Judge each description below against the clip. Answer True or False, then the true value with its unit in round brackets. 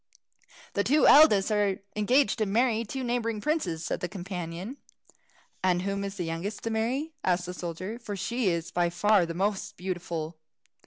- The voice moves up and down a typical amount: True (4.4 semitones)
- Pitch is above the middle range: True (200 Hz)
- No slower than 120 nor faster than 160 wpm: False (170 wpm)